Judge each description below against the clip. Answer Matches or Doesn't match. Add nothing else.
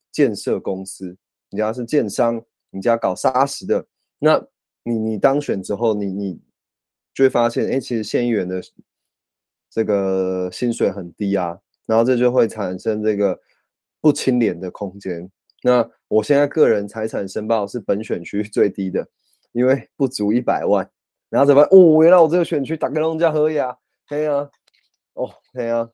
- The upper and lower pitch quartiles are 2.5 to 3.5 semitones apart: Doesn't match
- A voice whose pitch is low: Matches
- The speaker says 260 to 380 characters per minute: Doesn't match